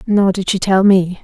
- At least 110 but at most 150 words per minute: No, fast, 245 wpm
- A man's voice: No, female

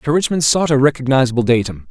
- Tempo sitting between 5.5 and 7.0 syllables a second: Yes, 6.6 syllables/s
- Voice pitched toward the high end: No, low, 135 Hz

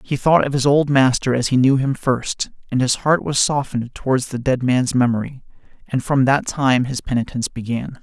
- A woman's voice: No, male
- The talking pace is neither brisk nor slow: No, fast, 210 wpm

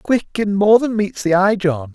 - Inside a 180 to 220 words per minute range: No, fast, 245 wpm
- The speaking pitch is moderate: No, high, 195 Hz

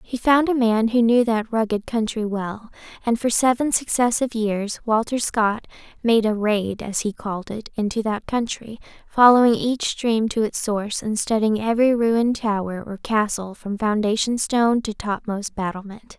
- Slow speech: No, average, 170 wpm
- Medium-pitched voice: No, high, 220 Hz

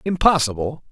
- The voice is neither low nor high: Yes, medium, 145 Hz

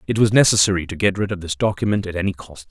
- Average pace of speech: No, fast, 265 wpm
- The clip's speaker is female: No, male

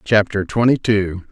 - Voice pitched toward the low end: Yes, low, 105 Hz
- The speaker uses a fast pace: No, slow, 135 wpm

